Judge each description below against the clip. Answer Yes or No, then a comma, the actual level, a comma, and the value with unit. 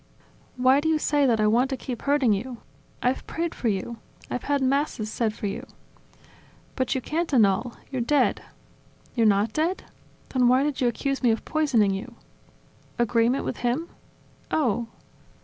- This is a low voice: No, very high, 250 Hz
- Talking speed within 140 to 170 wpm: No, average, 180 wpm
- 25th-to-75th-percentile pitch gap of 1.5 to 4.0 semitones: Yes, average, 3.7 semitones